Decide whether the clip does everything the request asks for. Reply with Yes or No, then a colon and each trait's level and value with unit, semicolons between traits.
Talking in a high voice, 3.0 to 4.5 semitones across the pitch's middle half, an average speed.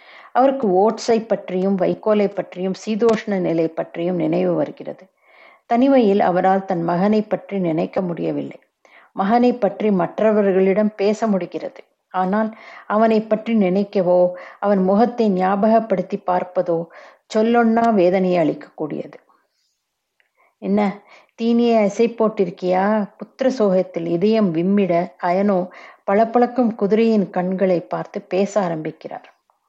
Yes: high, 200 Hz; average, 3.3 semitones; average, 95 wpm